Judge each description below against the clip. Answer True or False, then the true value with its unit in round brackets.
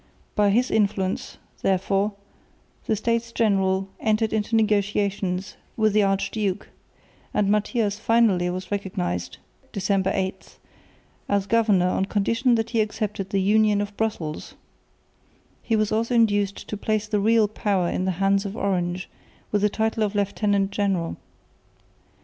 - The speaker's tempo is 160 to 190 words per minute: False (140 wpm)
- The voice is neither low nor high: False (205 Hz)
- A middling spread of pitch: False (2.0 semitones)